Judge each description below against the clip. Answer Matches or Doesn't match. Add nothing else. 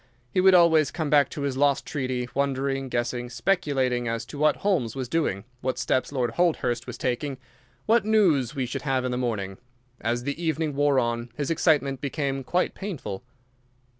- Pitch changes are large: Doesn't match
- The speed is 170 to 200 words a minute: Matches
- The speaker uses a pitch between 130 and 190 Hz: Matches